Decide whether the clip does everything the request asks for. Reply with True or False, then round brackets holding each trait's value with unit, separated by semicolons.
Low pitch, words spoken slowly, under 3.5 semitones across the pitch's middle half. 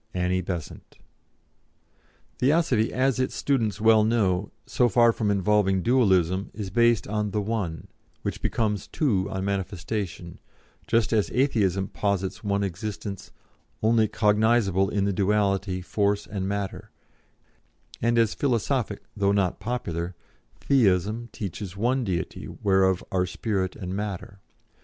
True (100 Hz; 125 wpm; 2.9 semitones)